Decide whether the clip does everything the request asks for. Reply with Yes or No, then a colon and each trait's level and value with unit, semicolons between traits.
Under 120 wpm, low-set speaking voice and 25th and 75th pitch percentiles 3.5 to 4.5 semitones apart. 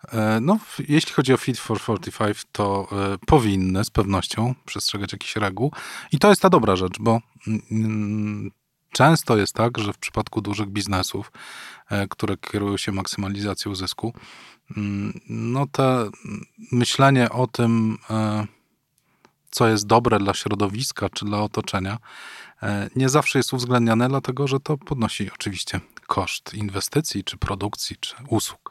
No: average, 145 wpm; low, 110 Hz; average, 3.8 semitones